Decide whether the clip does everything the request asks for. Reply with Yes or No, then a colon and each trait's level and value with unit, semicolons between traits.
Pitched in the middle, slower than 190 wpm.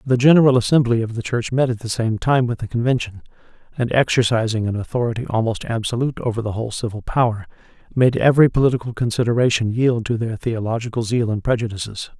No: low, 115 Hz; average, 175 wpm